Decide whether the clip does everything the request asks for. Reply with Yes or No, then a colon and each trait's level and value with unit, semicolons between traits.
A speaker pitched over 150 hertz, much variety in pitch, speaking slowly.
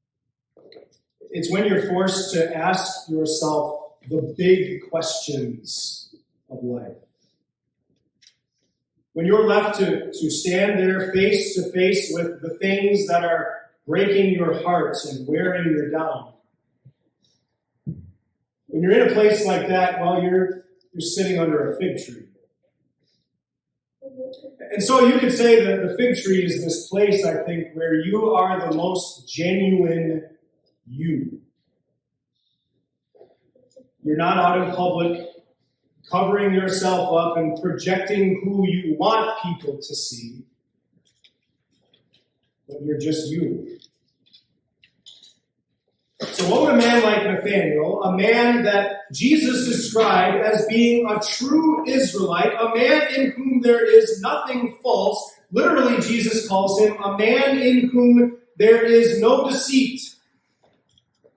Yes: high, 190 Hz; wide, 5.8 semitones; slow, 125 wpm